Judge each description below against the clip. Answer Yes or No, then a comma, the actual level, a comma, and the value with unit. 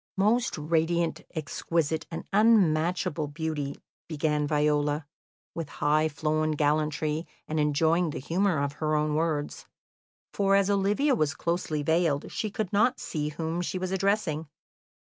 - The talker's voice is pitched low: No, medium, 160 Hz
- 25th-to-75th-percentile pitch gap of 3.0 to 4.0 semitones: Yes, average, 3.3 semitones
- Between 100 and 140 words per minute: Yes, slow, 135 wpm